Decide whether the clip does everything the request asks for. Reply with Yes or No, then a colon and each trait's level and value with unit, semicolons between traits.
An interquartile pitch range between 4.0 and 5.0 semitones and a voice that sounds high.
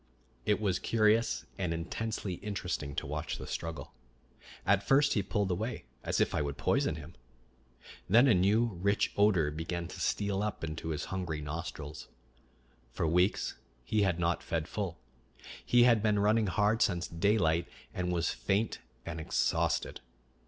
No: average, 4.3 semitones; very low, 95 Hz